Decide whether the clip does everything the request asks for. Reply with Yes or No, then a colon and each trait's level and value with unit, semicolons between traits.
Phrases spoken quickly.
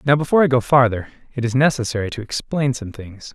Yes: fast, 215 wpm